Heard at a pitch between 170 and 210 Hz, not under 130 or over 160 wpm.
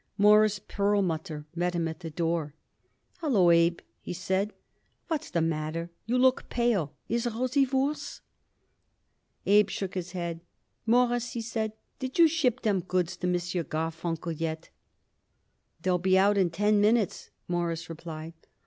Yes: medium, 185 Hz; average, 140 wpm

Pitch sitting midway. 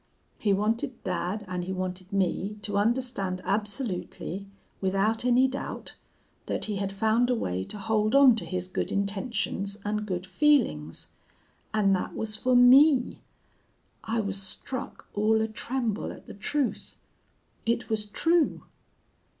No: high, 210 Hz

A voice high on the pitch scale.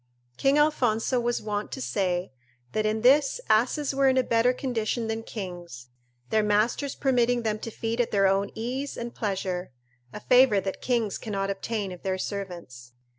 Yes: high, 220 Hz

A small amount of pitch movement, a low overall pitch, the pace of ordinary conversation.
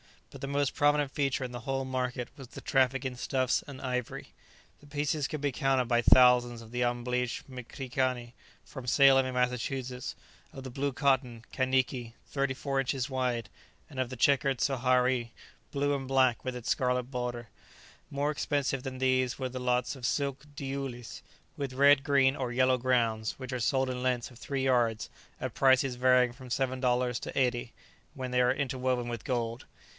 Yes: narrow, 1.6 semitones; low, 130 Hz; average, 180 wpm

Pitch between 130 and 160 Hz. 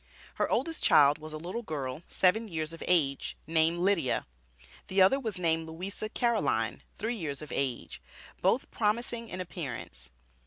No: medium, 170 Hz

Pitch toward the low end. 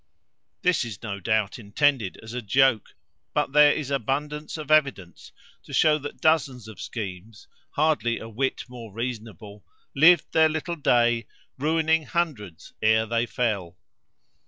Yes: low, 125 Hz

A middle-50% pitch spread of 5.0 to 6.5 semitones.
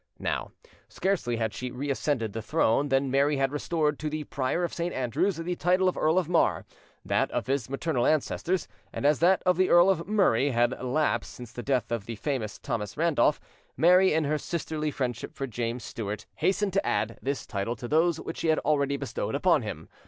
Yes: average, 5.3 semitones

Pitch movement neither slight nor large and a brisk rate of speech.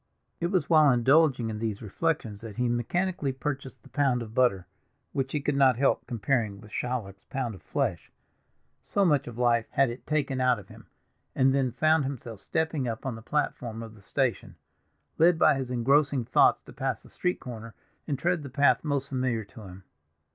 No: average, 3.9 semitones; average, 195 wpm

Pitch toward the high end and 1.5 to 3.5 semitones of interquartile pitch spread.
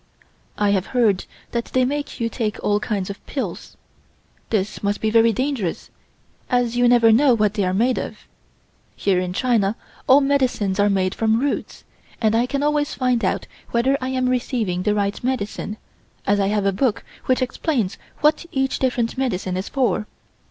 No: high, 230 Hz; average, 4.1 semitones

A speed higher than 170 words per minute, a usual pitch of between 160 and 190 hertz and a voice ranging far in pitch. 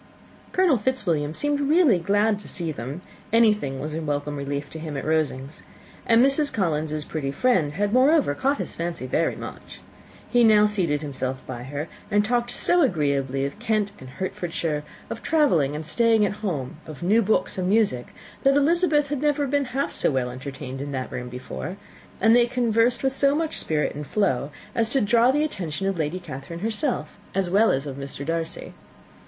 Yes: average, 185 wpm; medium, 185 Hz; wide, 8.6 semitones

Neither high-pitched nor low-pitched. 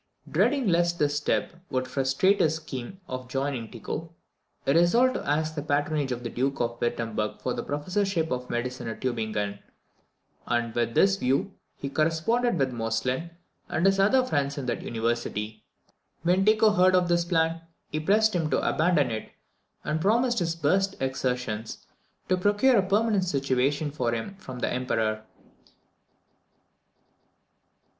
Yes: medium, 150 Hz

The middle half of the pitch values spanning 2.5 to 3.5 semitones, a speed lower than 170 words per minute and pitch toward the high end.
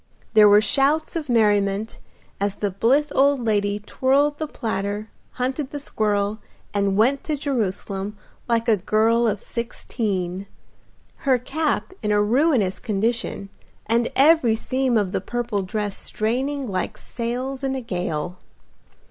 No: average, 4.6 semitones; average, 140 wpm; high, 225 Hz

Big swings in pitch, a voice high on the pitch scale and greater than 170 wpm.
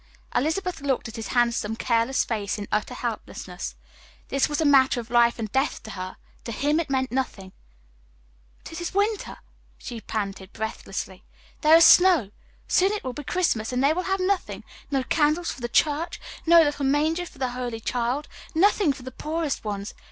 Yes: wide, 5.9 semitones; very high, 265 Hz; average, 185 wpm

